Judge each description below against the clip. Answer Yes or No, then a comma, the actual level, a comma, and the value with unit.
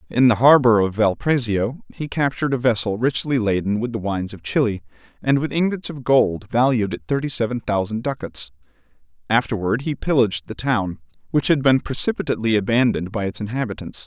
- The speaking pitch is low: Yes, low, 115 Hz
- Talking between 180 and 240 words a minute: No, average, 170 wpm